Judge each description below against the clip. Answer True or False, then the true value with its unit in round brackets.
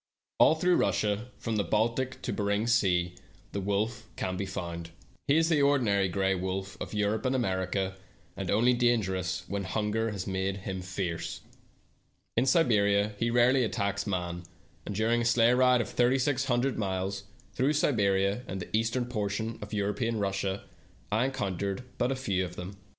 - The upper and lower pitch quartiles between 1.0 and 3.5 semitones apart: False (3.9 semitones)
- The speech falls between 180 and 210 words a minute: False (165 wpm)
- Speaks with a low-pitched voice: True (105 Hz)